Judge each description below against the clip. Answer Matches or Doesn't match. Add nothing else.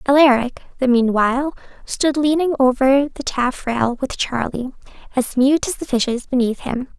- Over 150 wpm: Doesn't match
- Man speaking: Doesn't match